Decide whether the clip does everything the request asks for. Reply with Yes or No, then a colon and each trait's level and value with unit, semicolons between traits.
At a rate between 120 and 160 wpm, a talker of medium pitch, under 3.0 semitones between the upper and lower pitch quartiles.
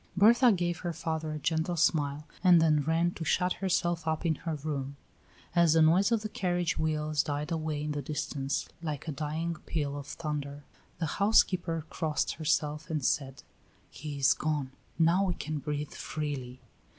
No: average, 175 wpm; medium, 155 Hz; narrow, 2.5 semitones